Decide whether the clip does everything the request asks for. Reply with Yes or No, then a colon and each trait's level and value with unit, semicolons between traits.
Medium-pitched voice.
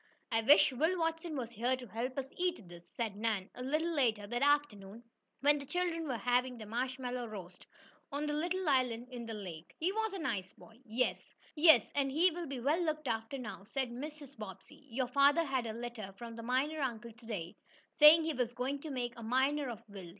No: very high, 255 Hz